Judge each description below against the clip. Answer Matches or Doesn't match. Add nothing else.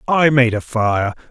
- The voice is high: Doesn't match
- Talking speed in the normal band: Matches